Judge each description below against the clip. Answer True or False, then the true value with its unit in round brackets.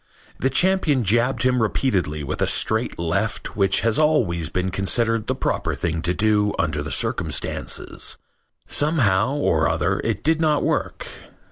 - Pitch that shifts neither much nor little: False (6.8 semitones)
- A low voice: True (110 Hz)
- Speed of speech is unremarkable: True (150 wpm)